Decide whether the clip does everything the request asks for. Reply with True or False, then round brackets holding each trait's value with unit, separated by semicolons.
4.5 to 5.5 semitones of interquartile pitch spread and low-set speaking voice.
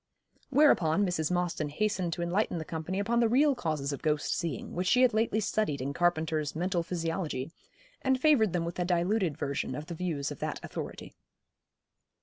False (5.1 semitones; 175 Hz)